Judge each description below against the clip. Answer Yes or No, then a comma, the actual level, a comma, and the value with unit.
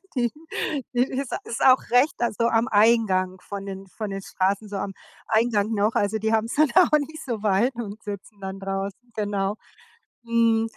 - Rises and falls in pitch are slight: No, average, 3.1 semitones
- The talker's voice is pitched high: Yes, high, 220 Hz